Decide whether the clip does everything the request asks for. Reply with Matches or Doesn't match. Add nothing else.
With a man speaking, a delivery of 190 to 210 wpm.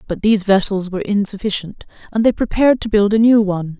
Doesn't match